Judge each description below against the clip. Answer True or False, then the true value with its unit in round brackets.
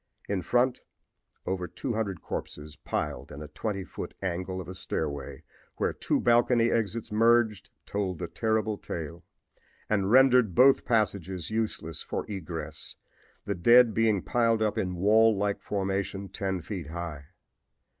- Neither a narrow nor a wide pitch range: True (4.2 semitones)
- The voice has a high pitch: False (100 Hz)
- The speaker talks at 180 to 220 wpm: False (140 wpm)